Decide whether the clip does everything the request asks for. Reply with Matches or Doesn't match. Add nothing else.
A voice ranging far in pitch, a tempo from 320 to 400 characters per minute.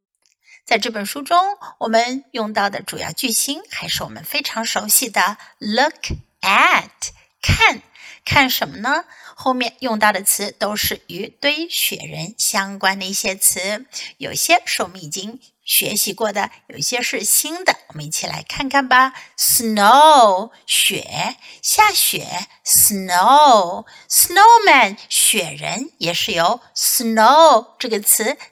Doesn't match